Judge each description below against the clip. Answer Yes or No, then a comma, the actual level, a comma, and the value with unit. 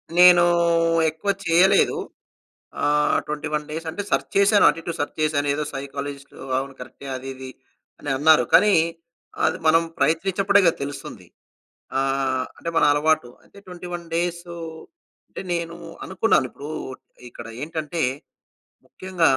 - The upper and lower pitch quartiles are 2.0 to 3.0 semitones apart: No, average, 3.4 semitones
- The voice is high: No, medium, 160 Hz